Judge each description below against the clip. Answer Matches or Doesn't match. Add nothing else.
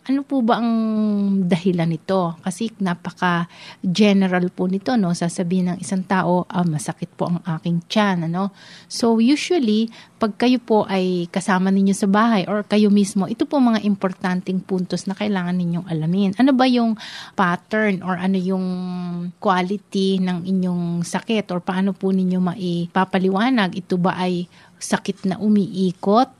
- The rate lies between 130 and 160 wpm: Matches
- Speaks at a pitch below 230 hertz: Matches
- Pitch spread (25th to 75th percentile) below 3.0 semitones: Matches